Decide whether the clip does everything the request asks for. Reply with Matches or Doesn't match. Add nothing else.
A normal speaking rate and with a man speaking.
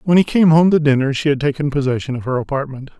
Doesn't match